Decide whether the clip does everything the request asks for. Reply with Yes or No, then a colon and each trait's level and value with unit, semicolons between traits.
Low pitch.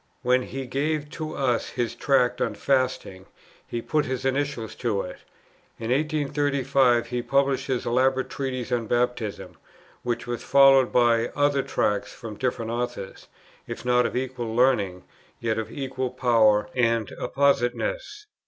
Yes: low, 125 Hz